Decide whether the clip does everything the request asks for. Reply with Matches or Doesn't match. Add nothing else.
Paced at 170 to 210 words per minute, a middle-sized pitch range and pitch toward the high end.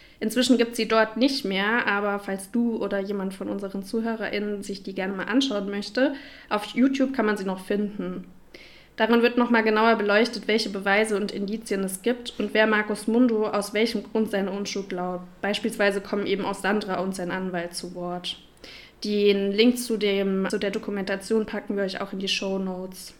Doesn't match